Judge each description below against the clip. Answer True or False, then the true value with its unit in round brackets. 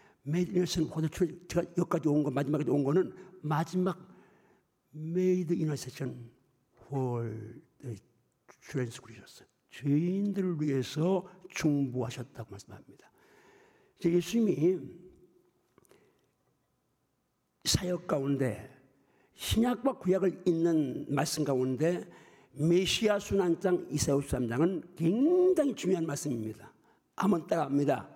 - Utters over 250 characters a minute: False (220 characters per minute)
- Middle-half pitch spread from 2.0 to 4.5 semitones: False (5.3 semitones)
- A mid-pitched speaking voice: True (160 Hz)